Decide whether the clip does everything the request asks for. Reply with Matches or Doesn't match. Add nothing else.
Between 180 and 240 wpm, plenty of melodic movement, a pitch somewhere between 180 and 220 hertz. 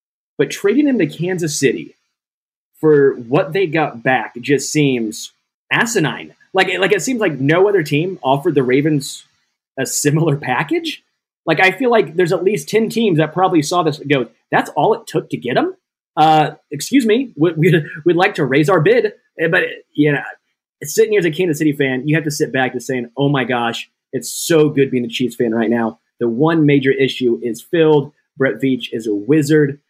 Doesn't match